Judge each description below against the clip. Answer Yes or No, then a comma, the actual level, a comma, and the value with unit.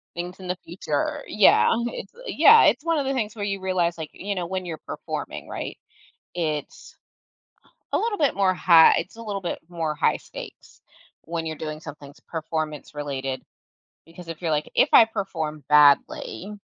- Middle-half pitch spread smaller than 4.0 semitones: No, average, 4.3 semitones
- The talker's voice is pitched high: No, medium, 170 Hz